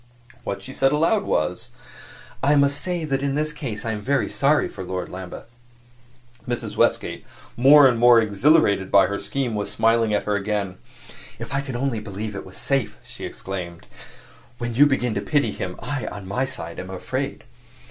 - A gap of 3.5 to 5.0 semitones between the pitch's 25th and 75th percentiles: No, wide, 5.5 semitones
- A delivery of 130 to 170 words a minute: No, average, 185 wpm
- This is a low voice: Yes, low, 120 Hz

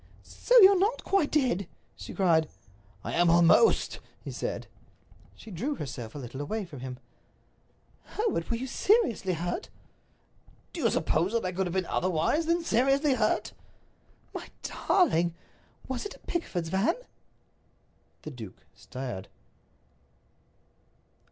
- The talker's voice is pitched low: No, high, 190 Hz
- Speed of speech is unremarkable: No, slow, 130 wpm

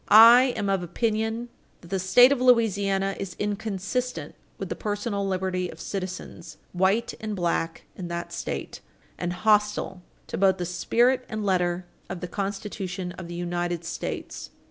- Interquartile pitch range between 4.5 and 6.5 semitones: No, average, 3.3 semitones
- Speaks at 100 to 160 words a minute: Yes, average, 155 wpm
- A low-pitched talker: No, high, 195 Hz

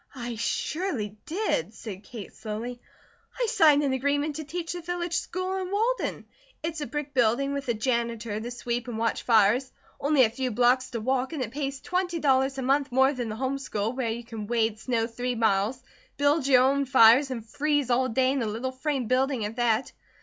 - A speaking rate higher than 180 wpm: Yes, fast, 205 wpm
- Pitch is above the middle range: Yes, very high, 255 Hz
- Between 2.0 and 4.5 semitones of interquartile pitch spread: Yes, average, 3.6 semitones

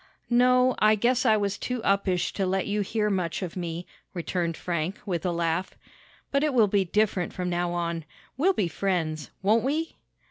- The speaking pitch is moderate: No, high, 195 Hz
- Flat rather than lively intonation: No, average, 4.0 semitones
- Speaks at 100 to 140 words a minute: No, average, 185 wpm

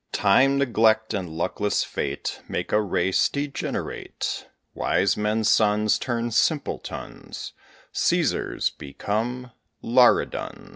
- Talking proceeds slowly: Yes, slow, 95 wpm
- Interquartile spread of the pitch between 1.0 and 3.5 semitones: Yes, average, 3.2 semitones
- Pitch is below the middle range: Yes, low, 110 Hz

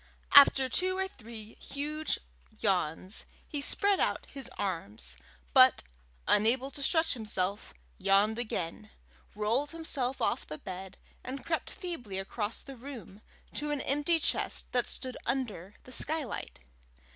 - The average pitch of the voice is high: Yes, very high, 250 Hz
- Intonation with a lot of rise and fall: Yes, wide, 6.1 semitones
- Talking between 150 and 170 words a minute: No, slow, 135 wpm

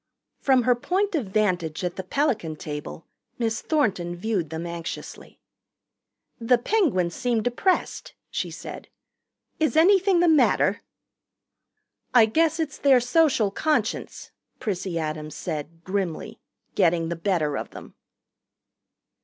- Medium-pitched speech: No, high, 215 Hz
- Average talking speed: No, slow, 120 wpm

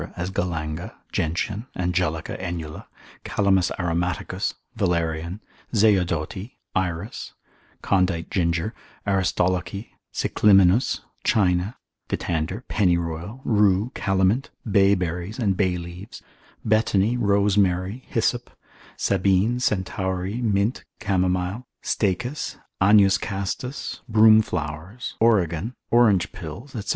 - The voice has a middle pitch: No, very low, 95 Hz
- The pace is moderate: No, slow, 90 wpm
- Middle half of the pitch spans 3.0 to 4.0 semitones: Yes, average, 3.3 semitones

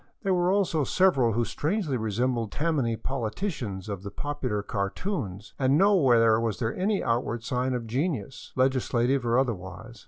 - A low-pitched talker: Yes, low, 125 Hz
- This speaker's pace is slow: No, average, 155 wpm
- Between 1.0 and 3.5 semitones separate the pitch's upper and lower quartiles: No, average, 4.8 semitones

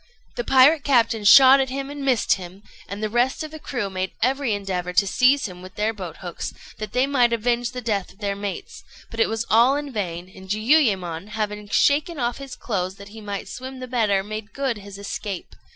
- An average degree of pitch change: Yes, average, 4.6 semitones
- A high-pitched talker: Yes, high, 220 Hz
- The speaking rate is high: Yes, fast, 215 wpm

